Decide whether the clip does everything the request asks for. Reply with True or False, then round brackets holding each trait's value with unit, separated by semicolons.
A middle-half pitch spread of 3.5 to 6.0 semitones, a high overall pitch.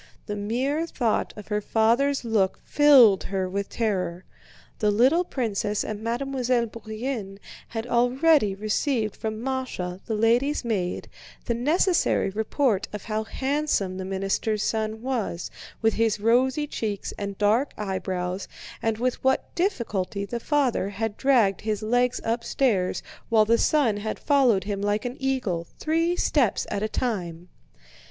True (4.1 semitones; 225 Hz)